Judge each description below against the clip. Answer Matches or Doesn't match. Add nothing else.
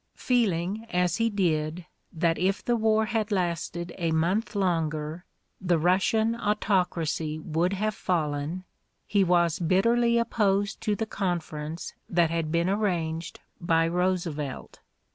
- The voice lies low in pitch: Doesn't match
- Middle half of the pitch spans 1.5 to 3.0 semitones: Doesn't match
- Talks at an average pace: Doesn't match